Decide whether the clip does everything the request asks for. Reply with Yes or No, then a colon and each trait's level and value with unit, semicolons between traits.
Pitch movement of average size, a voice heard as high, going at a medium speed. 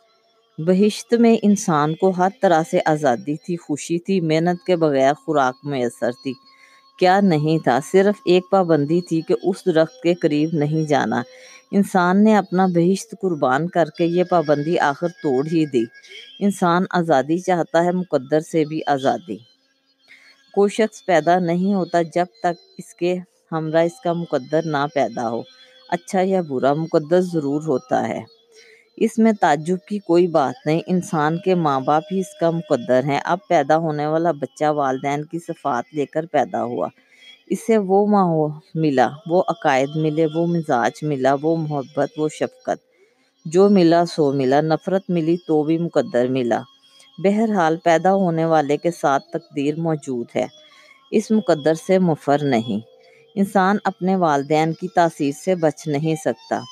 No: average, 3.9 semitones; medium, 170 Hz; average, 160 wpm